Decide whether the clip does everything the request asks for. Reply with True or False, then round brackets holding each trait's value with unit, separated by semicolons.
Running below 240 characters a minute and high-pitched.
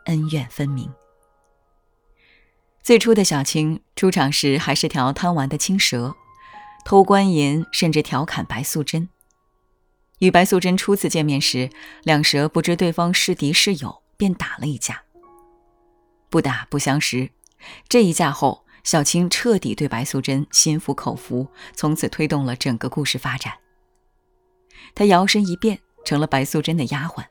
False (220 characters per minute; 155 Hz)